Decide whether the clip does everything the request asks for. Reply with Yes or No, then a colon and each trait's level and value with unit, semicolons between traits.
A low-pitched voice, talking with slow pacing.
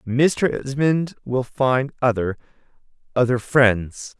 Yes: low, 130 Hz; slow, 85 wpm